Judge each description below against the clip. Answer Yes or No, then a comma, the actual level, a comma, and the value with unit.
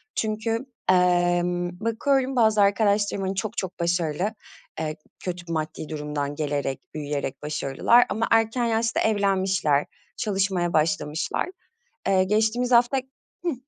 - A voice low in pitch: No, high, 190 Hz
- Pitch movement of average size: No, wide, 5.7 semitones